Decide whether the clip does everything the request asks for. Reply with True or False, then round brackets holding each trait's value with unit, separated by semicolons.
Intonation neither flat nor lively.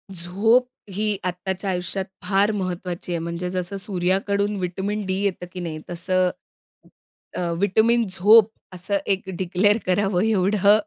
False (2.2 semitones)